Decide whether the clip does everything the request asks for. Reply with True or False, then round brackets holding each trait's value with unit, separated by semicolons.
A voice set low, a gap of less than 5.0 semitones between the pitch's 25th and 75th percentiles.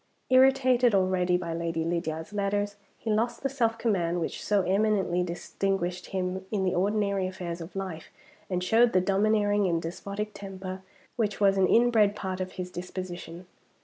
False (190 Hz; 2.7 semitones)